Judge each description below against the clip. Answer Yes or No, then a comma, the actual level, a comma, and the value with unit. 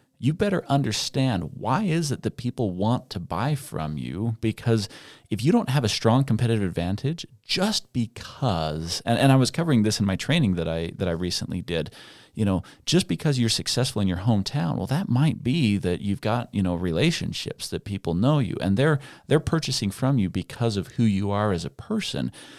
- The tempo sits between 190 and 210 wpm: Yes, average, 200 wpm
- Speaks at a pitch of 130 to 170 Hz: No, low, 115 Hz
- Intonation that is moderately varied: No, wide, 6.0 semitones